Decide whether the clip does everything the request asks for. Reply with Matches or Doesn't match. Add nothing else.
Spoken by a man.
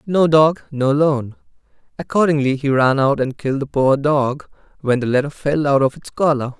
Matches